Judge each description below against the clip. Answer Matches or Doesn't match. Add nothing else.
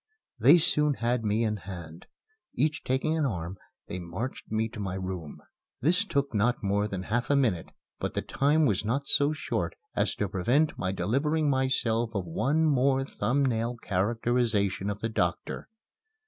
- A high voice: Doesn't match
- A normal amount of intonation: Doesn't match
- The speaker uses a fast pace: Doesn't match